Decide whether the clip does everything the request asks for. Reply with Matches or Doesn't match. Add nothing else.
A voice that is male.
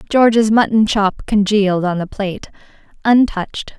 Doesn't match